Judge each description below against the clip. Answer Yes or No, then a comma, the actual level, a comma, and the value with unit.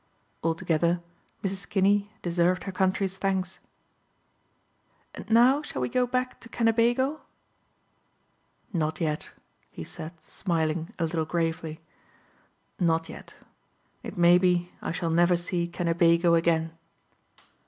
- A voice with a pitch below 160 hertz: No, medium, 175 Hz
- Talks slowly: Yes, slow, 115 wpm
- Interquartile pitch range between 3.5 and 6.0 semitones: No, average, 2.8 semitones